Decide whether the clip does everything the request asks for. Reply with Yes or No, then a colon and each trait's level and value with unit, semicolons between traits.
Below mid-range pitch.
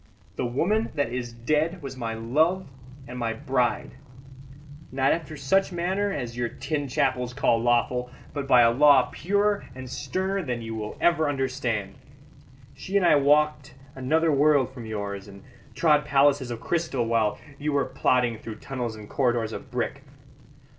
Yes: low, 130 Hz